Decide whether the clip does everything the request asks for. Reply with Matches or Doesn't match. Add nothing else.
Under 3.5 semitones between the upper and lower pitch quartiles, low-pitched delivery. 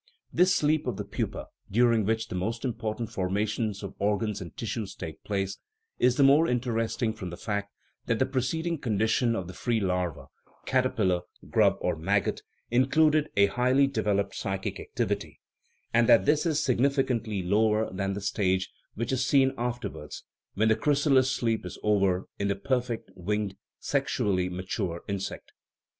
Doesn't match